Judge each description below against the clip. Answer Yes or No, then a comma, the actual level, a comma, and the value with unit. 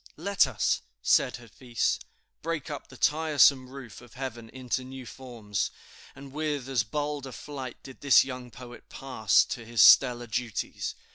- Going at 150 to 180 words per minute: Yes, average, 155 wpm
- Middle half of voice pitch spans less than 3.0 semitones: Yes, narrow, 2.5 semitones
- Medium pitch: No, low, 130 Hz